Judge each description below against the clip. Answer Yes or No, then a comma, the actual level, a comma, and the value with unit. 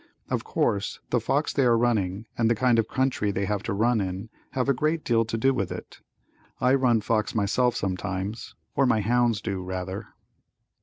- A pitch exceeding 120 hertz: No, low, 115 Hz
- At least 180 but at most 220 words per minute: Yes, average, 195 wpm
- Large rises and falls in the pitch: No, average, 3.7 semitones